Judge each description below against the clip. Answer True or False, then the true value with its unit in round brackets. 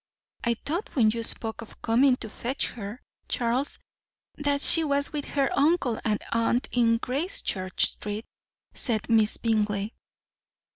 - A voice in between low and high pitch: False (235 Hz)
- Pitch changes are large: False (4.2 semitones)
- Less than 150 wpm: True (140 wpm)